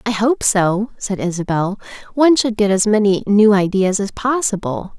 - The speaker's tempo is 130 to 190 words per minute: Yes, average, 170 wpm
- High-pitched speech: Yes, high, 205 Hz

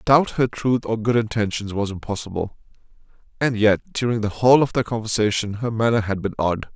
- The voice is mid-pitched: No, low, 110 Hz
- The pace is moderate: Yes, average, 195 wpm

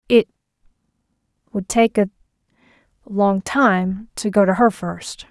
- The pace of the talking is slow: Yes, slow, 100 wpm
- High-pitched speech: Yes, high, 205 Hz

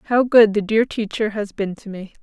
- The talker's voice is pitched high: Yes, high, 210 Hz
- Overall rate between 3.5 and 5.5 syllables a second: Yes, 4.7 syllables/s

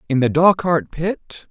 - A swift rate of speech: No, average, 160 wpm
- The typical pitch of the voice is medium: Yes, medium, 160 Hz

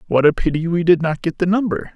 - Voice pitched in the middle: Yes, medium, 170 Hz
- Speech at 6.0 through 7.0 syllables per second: Yes, 6.2 syllables/s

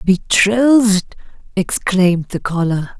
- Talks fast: No, slow, 80 wpm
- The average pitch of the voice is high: Yes, high, 195 Hz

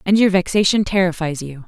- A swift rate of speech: No, average, 180 wpm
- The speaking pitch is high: No, medium, 180 Hz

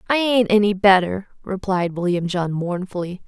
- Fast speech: No, average, 145 wpm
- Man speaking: No, female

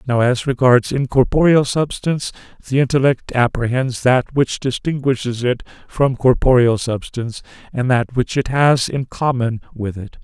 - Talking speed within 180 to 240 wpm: No, average, 140 wpm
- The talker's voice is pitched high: No, low, 125 Hz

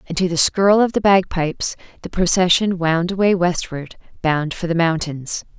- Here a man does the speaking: No, female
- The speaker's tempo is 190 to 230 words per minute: No, average, 170 wpm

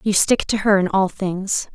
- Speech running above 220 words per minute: Yes, fast, 240 wpm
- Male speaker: No, female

